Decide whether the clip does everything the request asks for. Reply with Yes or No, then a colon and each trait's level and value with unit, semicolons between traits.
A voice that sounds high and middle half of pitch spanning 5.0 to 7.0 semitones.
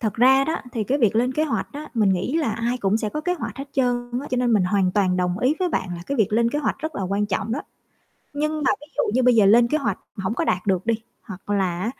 Yes: high, 235 Hz; wide, 5.5 semitones